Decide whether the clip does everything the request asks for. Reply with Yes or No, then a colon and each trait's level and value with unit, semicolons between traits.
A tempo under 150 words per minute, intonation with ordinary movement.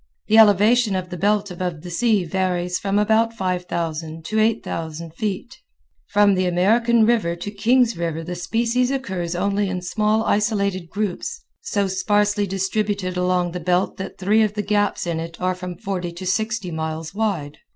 No: average, 170 wpm; average, 3.3 semitones